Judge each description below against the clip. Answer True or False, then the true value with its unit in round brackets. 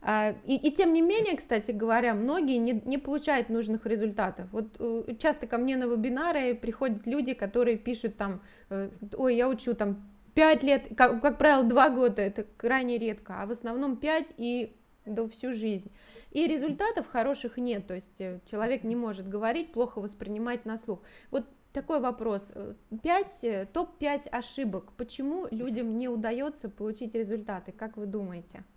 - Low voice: False (235 Hz)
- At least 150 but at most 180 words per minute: True (155 wpm)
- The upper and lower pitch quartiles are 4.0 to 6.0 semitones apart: False (3.6 semitones)